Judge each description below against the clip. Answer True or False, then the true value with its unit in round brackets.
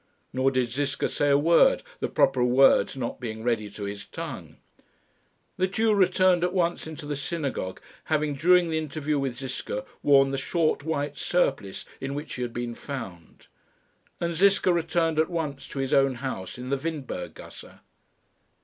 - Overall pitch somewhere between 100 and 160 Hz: True (140 Hz)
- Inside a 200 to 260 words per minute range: False (170 wpm)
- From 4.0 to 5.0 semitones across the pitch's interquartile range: True (4.4 semitones)